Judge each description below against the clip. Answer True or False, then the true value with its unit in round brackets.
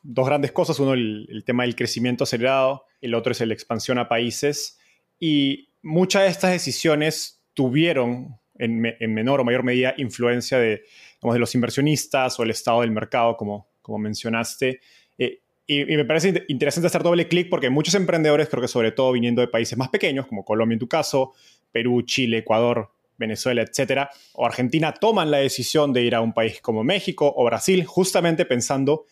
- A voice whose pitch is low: True (130 Hz)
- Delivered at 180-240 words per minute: True (190 wpm)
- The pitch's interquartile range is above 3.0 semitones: True (4.1 semitones)